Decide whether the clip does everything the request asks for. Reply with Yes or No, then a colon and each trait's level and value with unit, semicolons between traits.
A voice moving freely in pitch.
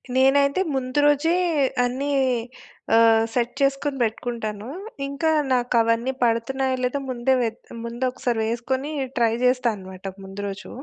No: average, 2.8 semitones